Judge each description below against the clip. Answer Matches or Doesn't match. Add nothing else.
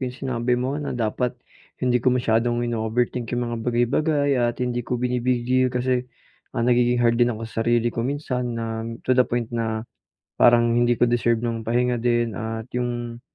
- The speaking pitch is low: Matches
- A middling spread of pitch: Doesn't match